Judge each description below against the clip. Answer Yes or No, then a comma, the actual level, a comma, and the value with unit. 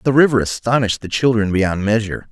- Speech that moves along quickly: No, average, 180 wpm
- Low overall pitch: Yes, low, 115 Hz